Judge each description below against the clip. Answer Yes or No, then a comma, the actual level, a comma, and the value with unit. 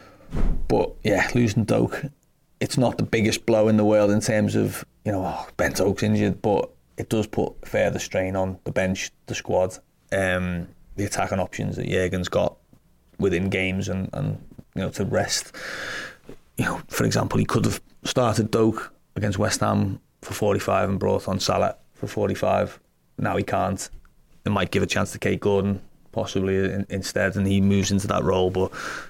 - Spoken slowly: No, average, 180 wpm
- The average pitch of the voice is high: No, low, 100 Hz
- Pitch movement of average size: No, narrow, 2.0 semitones